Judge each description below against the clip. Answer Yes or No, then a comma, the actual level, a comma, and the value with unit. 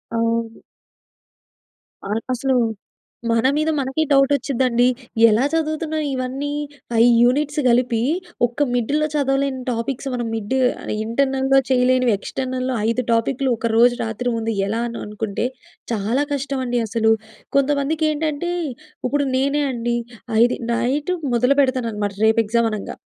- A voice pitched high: Yes, very high, 255 Hz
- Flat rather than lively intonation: No, average, 3.2 semitones